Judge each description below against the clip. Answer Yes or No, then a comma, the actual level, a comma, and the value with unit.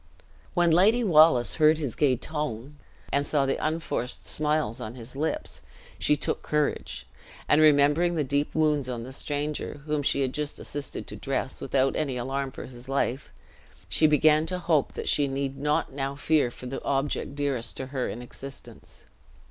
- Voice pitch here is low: No, medium, 145 Hz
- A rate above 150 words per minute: Yes, average, 175 wpm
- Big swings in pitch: No, narrow, 2.4 semitones